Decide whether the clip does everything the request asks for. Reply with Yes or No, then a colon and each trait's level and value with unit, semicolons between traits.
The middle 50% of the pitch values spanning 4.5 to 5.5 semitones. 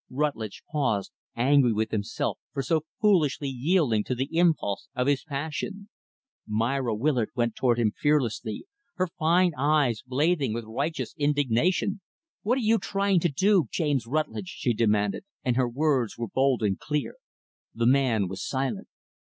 Yes: average, 5.0 semitones